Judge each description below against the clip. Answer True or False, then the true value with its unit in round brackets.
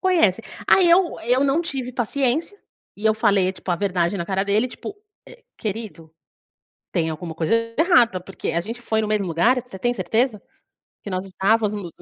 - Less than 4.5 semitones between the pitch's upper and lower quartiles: False (5.1 semitones)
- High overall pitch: True (215 Hz)